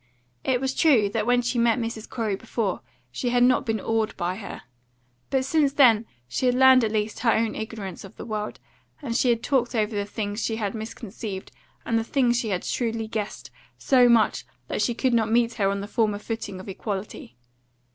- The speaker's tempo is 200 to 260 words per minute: Yes, fast, 205 wpm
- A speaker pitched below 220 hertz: No, high, 225 Hz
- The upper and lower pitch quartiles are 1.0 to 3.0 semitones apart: Yes, narrow, 2.6 semitones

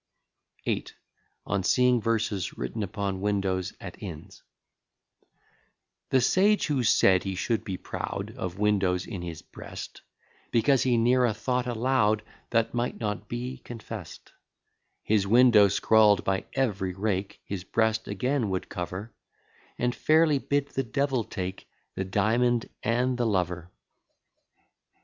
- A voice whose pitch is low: Yes, low, 110 Hz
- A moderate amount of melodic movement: Yes, average, 4.2 semitones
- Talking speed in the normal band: No, slow, 130 wpm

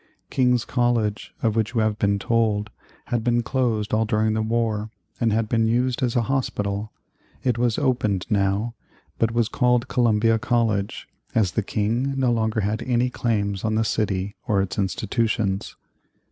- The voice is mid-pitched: No, low, 110 Hz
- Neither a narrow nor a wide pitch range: No, narrow, 2.2 semitones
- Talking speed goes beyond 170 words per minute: No, average, 165 wpm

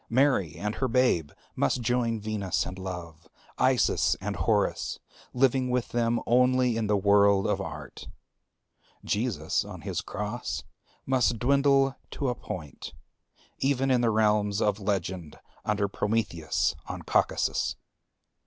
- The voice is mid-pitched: No, low, 110 Hz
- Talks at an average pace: No, slow, 130 wpm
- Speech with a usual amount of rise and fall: Yes, average, 4.1 semitones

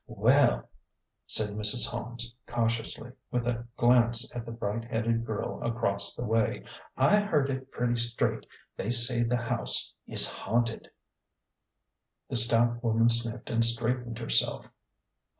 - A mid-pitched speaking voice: No, low, 120 Hz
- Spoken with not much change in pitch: Yes, narrow, 0.9 semitones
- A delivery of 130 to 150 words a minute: Yes, average, 140 wpm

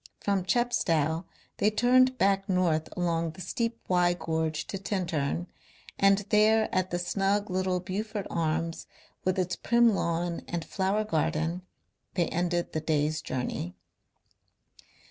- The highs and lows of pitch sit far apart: No, average, 3.5 semitones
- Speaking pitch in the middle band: Yes, medium, 180 Hz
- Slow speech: Yes, slow, 130 wpm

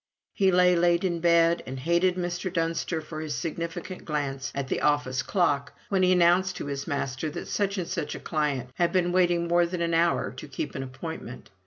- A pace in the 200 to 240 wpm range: Yes, fast, 205 wpm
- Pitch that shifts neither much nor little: Yes, average, 3.3 semitones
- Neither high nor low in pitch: Yes, medium, 170 Hz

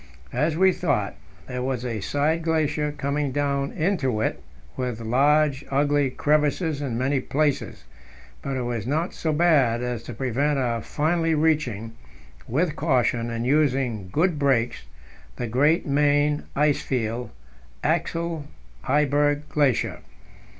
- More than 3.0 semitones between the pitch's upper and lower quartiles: Yes, average, 3.5 semitones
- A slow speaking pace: Yes, slow, 130 wpm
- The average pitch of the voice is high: No, medium, 140 Hz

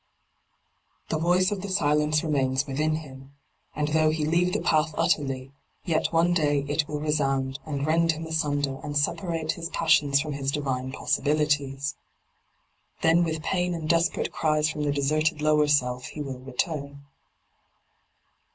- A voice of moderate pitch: Yes, medium, 150 Hz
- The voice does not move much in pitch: Yes, narrow, 2.3 semitones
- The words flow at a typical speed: Yes, average, 150 wpm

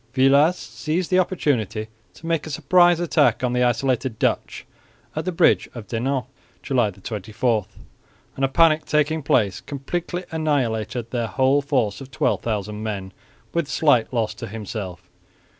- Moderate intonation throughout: No, wide, 5.7 semitones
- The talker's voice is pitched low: Yes, low, 130 Hz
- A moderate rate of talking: Yes, average, 145 wpm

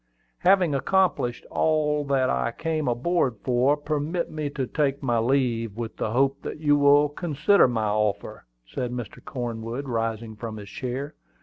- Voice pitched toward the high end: No, low, 135 Hz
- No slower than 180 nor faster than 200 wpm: No, average, 165 wpm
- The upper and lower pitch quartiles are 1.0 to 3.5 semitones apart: No, average, 4.3 semitones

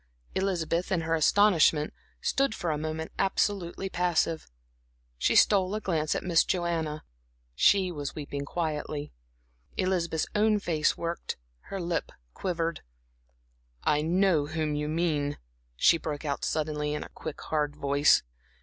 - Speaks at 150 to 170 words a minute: No, slow, 135 wpm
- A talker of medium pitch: Yes, medium, 165 Hz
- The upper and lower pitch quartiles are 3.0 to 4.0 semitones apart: Yes, average, 3.3 semitones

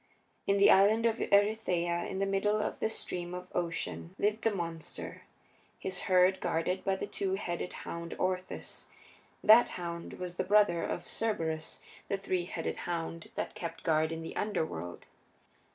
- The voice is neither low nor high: Yes, medium, 180 Hz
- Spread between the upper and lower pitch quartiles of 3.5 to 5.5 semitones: No, average, 3.0 semitones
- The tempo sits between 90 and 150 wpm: No, average, 160 wpm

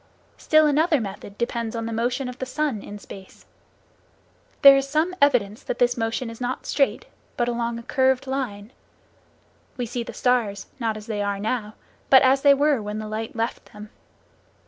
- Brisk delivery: No, average, 185 wpm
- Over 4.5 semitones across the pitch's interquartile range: No, average, 3.6 semitones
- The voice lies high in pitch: Yes, high, 240 Hz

